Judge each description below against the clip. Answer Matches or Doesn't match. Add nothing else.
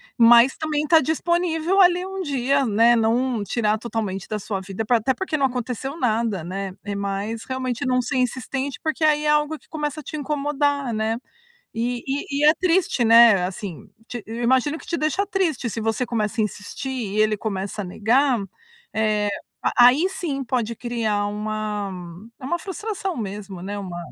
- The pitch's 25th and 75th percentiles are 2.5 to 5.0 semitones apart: Doesn't match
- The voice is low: Doesn't match